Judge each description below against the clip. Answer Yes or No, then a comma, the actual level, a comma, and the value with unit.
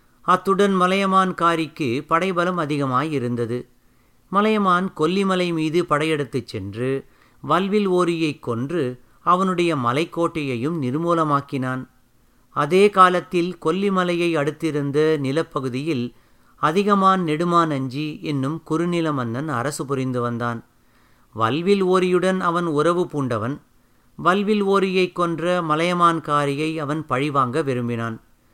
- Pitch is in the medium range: Yes, medium, 155 Hz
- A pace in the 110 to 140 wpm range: No, average, 90 wpm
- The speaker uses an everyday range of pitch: Yes, average, 5.0 semitones